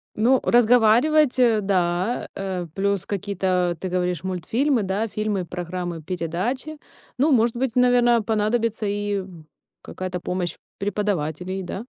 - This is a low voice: No, high, 200 Hz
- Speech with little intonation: No, average, 4.4 semitones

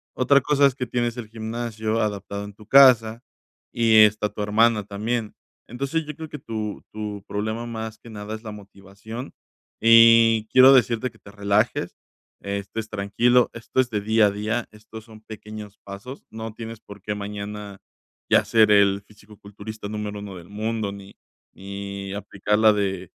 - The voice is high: No, low, 110 Hz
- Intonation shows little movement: Yes, narrow, 2.1 semitones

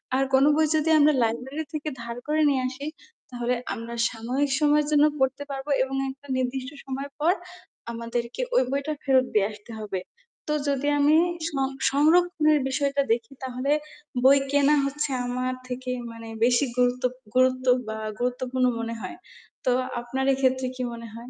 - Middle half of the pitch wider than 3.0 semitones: No, average, 2.7 semitones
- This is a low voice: No, very high, 260 Hz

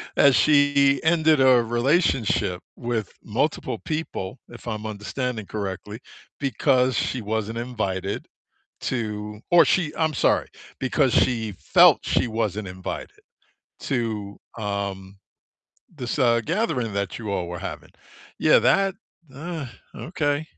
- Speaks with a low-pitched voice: Yes, low, 120 Hz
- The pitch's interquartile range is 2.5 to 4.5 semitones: No, average, 5.2 semitones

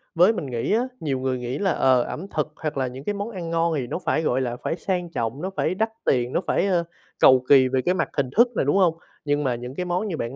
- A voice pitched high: No, medium, 150 Hz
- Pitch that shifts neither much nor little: No, wide, 5.8 semitones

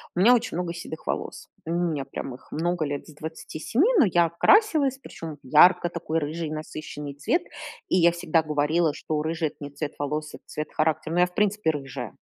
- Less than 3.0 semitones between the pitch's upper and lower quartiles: Yes, narrow, 2.6 semitones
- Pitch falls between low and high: Yes, medium, 160 Hz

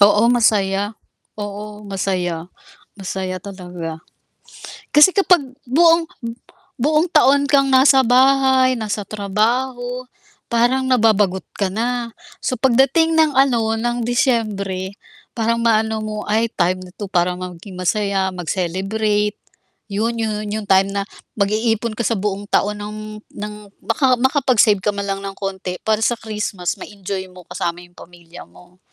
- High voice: Yes, high, 210 Hz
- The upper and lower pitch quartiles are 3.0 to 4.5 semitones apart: Yes, average, 3.9 semitones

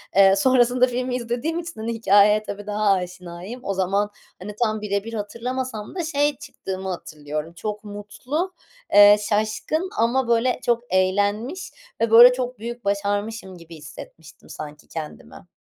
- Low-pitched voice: No, high, 210 Hz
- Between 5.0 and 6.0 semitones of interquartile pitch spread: No, average, 4.1 semitones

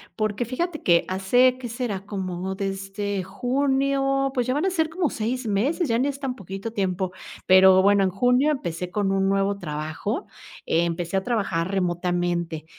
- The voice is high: Yes, high, 200 Hz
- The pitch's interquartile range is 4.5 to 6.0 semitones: Yes, wide, 5.4 semitones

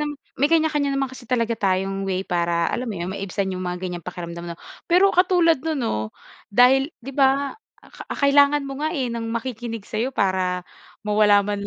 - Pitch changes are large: Yes, wide, 6.6 semitones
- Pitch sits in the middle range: No, high, 230 Hz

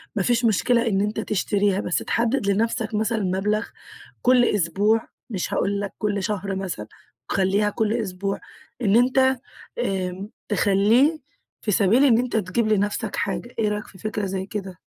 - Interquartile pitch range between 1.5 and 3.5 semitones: Yes, average, 2.7 semitones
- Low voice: No, high, 210 Hz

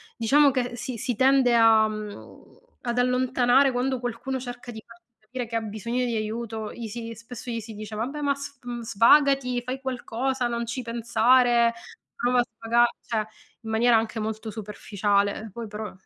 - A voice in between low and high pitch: No, high, 235 Hz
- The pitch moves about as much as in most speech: No, narrow, 2.2 semitones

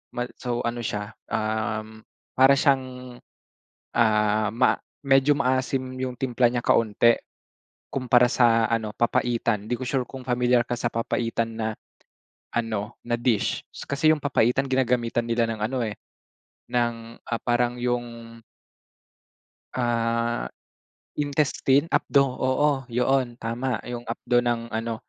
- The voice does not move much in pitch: Yes, narrow, 1.9 semitones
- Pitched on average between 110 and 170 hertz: Yes, low, 120 Hz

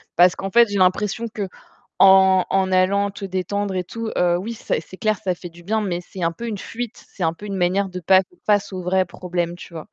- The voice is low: No, high, 190 Hz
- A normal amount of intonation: No, narrow, 2.2 semitones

